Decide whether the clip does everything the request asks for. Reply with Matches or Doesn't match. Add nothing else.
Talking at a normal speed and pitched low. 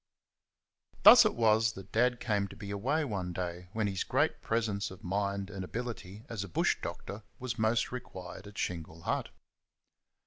Matches